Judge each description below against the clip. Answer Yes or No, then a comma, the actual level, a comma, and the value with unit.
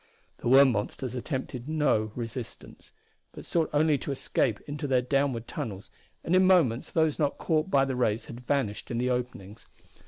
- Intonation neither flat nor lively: Yes, average, 3.9 semitones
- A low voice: Yes, low, 130 Hz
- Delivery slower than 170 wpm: No, average, 175 wpm